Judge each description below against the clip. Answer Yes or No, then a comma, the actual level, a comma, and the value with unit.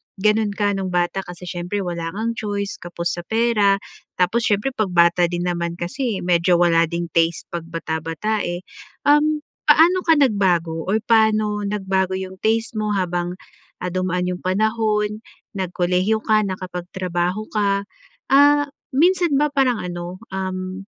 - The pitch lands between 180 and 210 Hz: Yes, high, 190 Hz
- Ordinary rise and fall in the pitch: Yes, average, 3.7 semitones